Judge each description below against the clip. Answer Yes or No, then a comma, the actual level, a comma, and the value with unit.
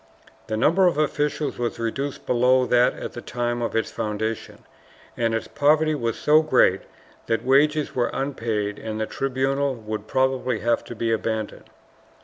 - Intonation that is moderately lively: Yes, average, 3.7 semitones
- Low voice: Yes, low, 120 Hz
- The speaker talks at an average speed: Yes, average, 160 wpm